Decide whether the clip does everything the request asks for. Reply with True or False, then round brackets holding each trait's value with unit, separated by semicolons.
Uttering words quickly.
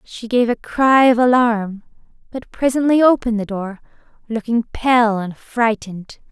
False (145 wpm)